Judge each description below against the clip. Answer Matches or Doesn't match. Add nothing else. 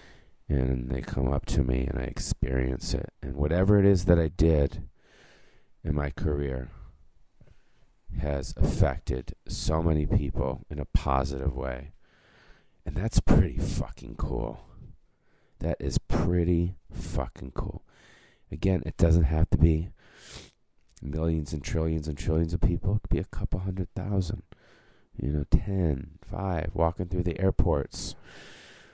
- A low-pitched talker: Matches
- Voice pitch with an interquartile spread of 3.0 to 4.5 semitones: Matches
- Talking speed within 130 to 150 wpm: Matches